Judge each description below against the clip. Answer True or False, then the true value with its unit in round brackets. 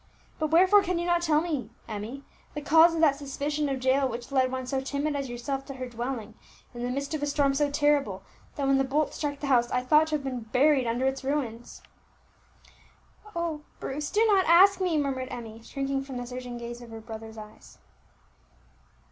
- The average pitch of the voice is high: True (275 Hz)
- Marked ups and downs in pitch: False (3.5 semitones)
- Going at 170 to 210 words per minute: True (205 wpm)